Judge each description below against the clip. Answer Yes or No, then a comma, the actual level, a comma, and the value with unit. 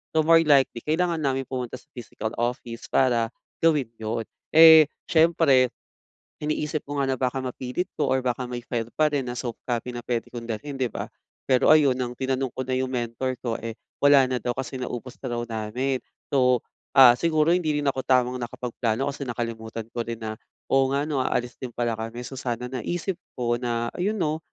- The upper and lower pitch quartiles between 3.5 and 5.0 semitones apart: No, average, 3.0 semitones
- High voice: No, low, 130 Hz